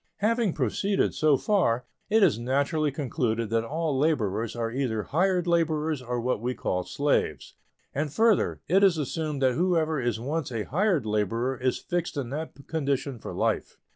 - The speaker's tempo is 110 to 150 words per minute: No, average, 170 wpm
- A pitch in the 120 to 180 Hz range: Yes, medium, 140 Hz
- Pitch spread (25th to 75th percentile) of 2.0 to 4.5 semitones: No, average, 5.3 semitones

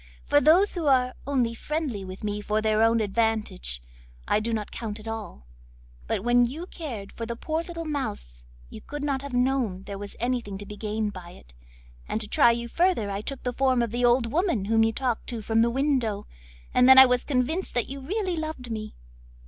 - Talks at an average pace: No, fast, 215 wpm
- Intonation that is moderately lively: Yes, average, 4.3 semitones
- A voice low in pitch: No, high, 235 Hz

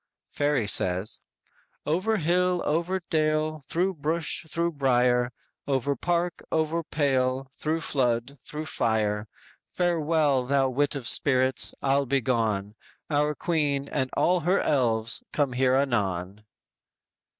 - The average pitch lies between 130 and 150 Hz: Yes, medium, 140 Hz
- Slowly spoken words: Yes, slow, 125 wpm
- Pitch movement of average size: Yes, average, 4.3 semitones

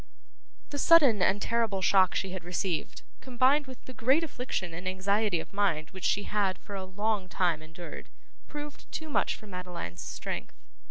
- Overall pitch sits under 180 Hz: No, high, 200 Hz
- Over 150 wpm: Yes, average, 170 wpm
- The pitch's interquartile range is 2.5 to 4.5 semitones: No, average, 5.2 semitones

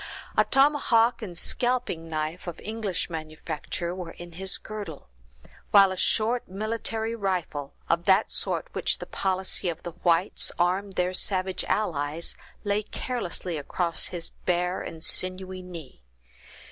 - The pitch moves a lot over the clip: No, average, 3.5 semitones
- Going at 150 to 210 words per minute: No, average, 140 wpm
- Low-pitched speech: No, medium, 185 Hz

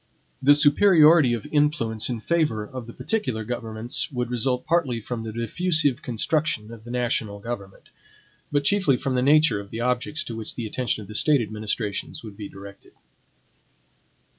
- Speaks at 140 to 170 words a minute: Yes, average, 165 wpm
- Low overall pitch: Yes, low, 120 Hz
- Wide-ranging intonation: No, average, 4.8 semitones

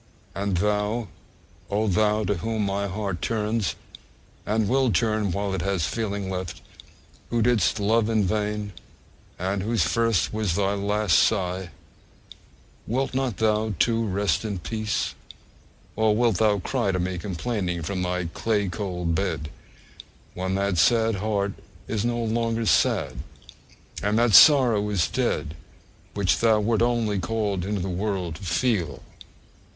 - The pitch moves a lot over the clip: No, average, 3.0 semitones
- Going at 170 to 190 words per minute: No, average, 145 wpm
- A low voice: Yes, low, 105 Hz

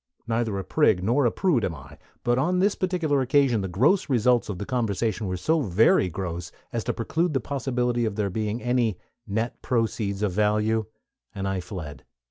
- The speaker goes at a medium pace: Yes, average, 190 wpm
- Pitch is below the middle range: Yes, low, 115 Hz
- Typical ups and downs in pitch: Yes, average, 4.7 semitones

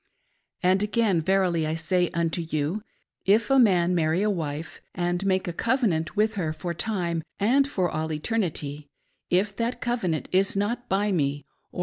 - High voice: No, medium, 180 Hz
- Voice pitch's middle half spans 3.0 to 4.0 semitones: No, average, 4.5 semitones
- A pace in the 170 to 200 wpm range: Yes, average, 180 wpm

